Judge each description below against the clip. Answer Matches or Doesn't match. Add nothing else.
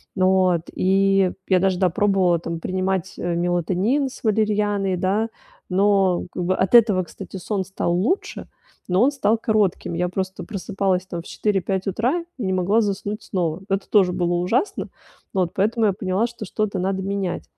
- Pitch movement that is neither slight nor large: Doesn't match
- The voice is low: Doesn't match